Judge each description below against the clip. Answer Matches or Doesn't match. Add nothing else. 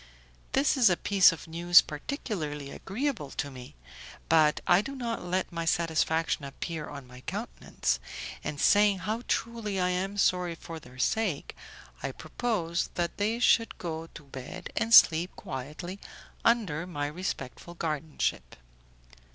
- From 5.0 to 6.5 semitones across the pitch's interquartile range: Matches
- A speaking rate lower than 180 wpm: Matches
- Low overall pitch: Doesn't match